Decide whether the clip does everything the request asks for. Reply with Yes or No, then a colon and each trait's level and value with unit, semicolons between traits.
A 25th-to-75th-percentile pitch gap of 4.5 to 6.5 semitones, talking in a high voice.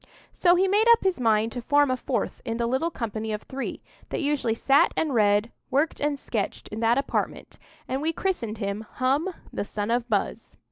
Yes: average, 4.8 semitones; very high, 250 Hz